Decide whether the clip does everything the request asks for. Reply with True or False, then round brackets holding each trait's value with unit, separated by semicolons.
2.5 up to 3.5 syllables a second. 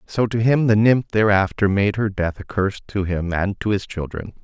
False (5.2 syllables/s)